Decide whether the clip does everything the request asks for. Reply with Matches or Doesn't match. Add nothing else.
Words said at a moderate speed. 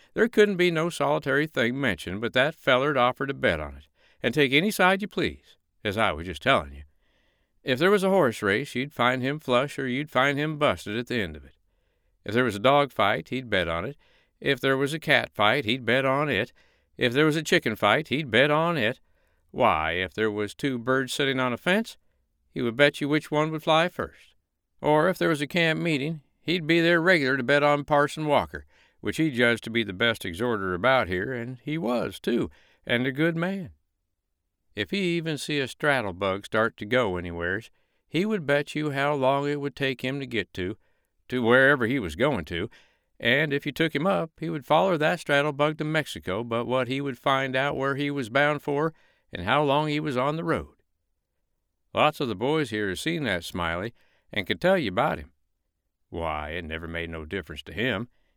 Doesn't match